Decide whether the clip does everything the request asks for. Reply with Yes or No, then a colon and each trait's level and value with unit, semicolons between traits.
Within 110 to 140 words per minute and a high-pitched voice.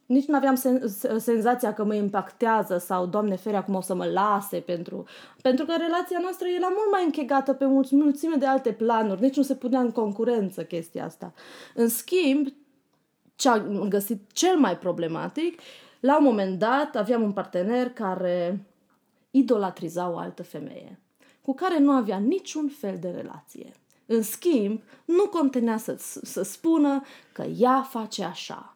No: average, 155 wpm; high, 245 Hz